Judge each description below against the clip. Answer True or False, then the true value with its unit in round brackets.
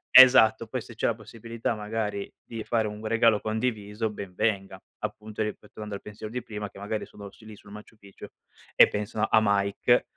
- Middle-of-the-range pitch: False (110 Hz)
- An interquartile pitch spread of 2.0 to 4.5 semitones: False (1.4 semitones)